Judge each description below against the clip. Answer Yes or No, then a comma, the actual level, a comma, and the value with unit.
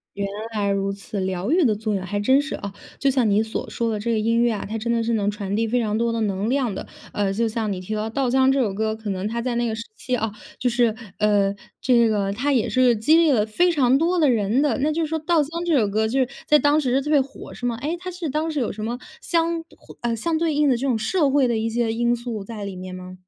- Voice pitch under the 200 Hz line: No, high, 230 Hz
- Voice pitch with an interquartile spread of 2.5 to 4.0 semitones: No, average, 4.5 semitones